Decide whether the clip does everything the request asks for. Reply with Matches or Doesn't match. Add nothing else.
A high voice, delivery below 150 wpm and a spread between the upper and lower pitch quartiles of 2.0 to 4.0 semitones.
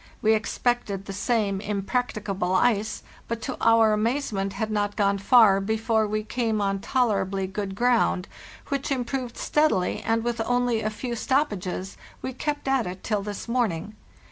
Doesn't match